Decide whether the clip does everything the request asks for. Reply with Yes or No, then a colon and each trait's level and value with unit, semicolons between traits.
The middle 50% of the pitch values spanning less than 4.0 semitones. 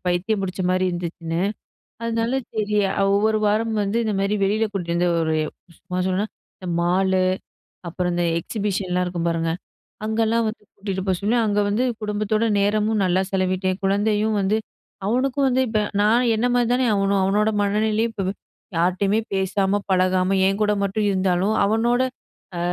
Yes: average, 2.8 semitones